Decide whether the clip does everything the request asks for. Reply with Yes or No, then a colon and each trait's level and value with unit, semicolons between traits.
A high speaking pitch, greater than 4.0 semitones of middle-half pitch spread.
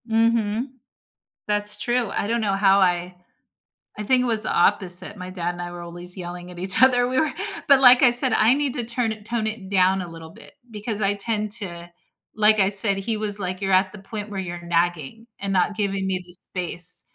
No: high, 200 Hz; average, 3.7 semitones